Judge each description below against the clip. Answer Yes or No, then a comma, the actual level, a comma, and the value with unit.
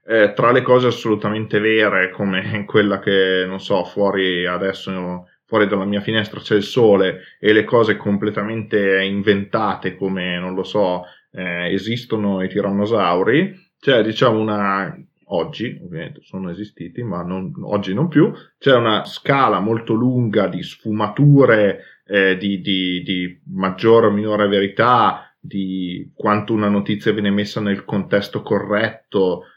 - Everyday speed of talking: Yes, average, 145 wpm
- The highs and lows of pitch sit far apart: No, narrow, 2.4 semitones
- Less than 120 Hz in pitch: Yes, low, 100 Hz